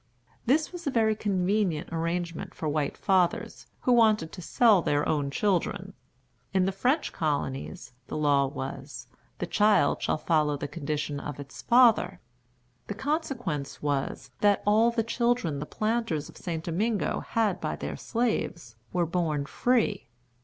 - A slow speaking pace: No, average, 150 wpm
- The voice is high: No, medium, 180 Hz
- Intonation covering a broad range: Yes, wide, 6.8 semitones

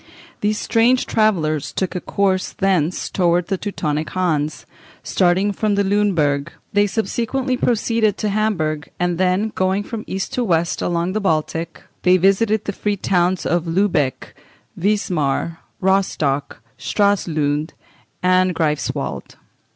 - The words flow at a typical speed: No, slow, 125 wpm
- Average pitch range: Yes, average, 3.9 semitones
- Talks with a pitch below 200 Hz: Yes, medium, 185 Hz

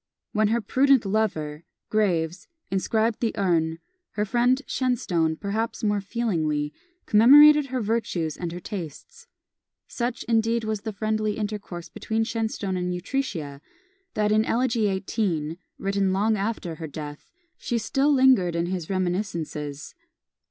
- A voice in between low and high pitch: No, high, 210 Hz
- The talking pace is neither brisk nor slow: No, slow, 130 wpm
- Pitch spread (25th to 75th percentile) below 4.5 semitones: No, average, 4.8 semitones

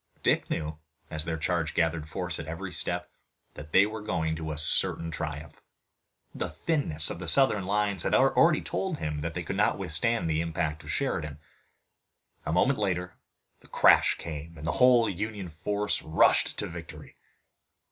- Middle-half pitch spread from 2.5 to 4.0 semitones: No, average, 4.7 semitones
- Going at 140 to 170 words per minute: Yes, average, 165 wpm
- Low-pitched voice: Yes, very low, 85 Hz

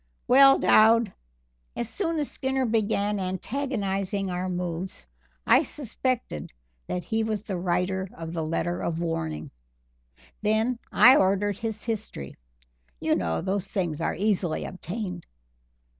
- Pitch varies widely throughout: No, average, 4.2 semitones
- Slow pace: Yes, slow, 130 wpm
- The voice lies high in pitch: Yes, high, 195 Hz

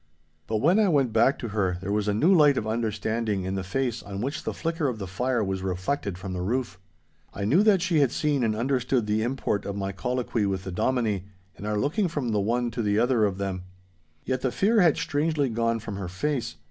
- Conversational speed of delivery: No, fast, 235 wpm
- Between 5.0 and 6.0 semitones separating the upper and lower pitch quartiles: Yes, average, 5.3 semitones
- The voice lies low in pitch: Yes, low, 115 Hz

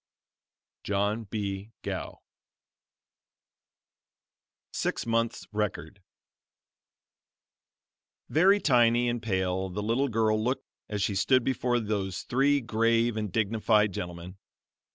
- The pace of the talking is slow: Yes, slow, 95 wpm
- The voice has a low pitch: Yes, low, 110 Hz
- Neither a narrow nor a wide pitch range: Yes, average, 3.0 semitones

